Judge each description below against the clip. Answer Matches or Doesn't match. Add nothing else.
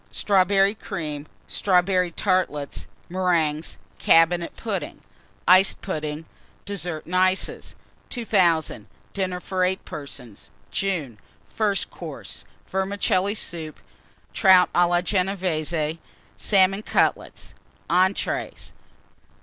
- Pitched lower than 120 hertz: Doesn't match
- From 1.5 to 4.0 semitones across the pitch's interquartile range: Matches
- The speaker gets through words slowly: Matches